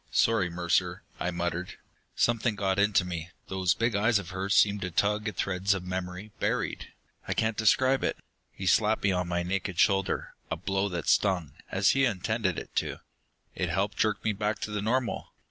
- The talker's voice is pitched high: No, low, 100 Hz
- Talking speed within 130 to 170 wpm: No, average, 195 wpm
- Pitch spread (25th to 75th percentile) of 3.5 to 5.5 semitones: No, average, 2.9 semitones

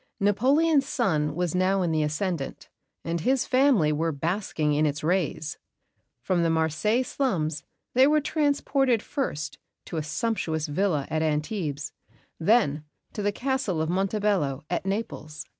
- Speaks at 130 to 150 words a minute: Yes, average, 140 wpm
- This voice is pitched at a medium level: Yes, medium, 180 Hz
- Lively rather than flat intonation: Yes, wide, 6.9 semitones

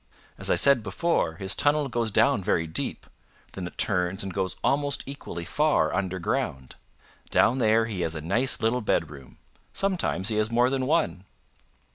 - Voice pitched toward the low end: Yes, low, 110 Hz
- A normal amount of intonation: No, wide, 6.7 semitones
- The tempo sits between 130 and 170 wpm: Yes, average, 165 wpm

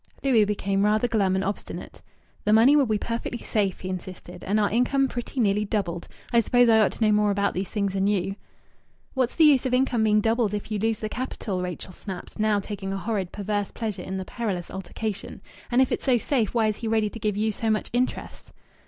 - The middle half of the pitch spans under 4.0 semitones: Yes, average, 2.8 semitones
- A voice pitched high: Yes, high, 215 Hz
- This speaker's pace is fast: Yes, fast, 225 wpm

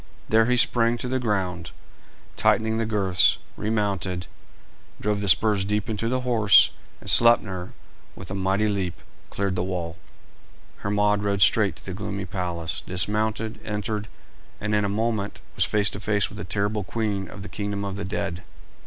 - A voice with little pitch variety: Yes, narrow, 2.2 semitones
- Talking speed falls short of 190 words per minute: Yes, average, 170 wpm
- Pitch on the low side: Yes, low, 100 Hz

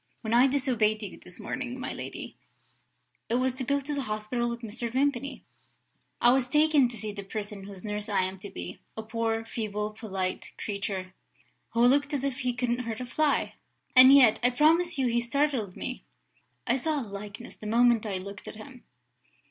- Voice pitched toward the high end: Yes, high, 235 Hz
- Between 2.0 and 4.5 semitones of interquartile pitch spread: Yes, average, 3.7 semitones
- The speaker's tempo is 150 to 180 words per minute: No, average, 195 wpm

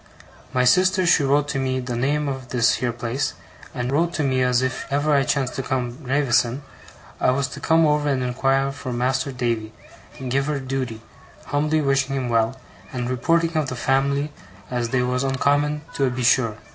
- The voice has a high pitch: No, low, 135 Hz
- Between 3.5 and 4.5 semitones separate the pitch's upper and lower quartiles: No, narrow, 2.4 semitones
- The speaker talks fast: No, average, 195 wpm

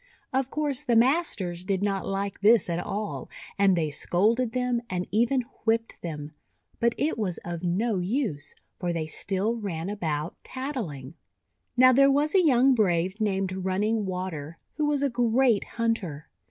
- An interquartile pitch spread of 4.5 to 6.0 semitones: Yes, wide, 5.5 semitones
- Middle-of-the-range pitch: No, high, 205 Hz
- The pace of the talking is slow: No, average, 165 wpm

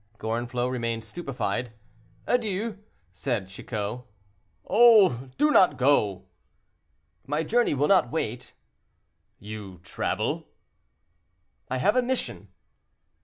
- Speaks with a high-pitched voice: No, low, 130 Hz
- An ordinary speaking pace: No, slow, 95 wpm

